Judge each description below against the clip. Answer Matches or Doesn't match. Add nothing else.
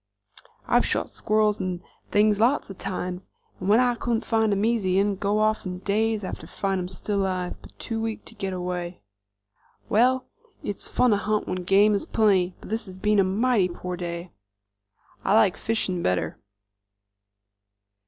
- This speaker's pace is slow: Doesn't match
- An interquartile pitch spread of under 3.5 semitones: Matches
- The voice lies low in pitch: Doesn't match